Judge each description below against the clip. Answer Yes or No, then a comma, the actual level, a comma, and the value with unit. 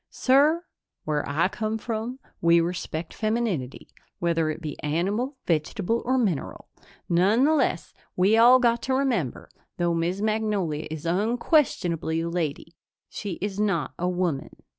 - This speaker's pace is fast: No, slow, 135 wpm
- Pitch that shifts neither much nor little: No, wide, 5.8 semitones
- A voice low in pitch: No, medium, 185 Hz